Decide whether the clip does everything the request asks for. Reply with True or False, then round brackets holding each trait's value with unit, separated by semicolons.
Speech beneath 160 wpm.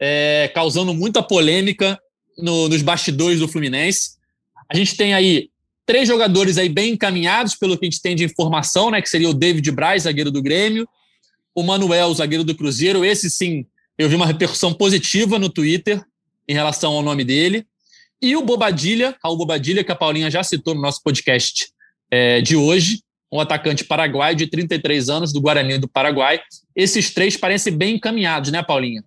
False (180 wpm)